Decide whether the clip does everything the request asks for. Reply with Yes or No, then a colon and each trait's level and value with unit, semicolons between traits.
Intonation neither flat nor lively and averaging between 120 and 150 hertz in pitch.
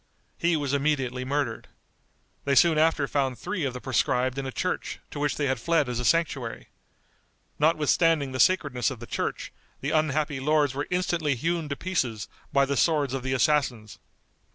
Yes: average, 3.1 semitones; medium, 140 Hz